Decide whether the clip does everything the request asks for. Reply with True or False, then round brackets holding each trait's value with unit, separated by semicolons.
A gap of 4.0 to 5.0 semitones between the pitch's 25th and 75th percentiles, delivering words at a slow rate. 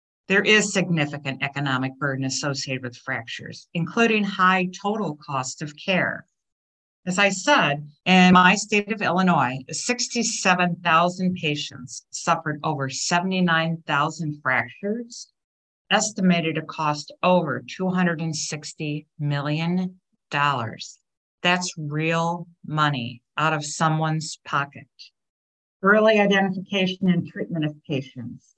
True (4.5 semitones; 100 wpm)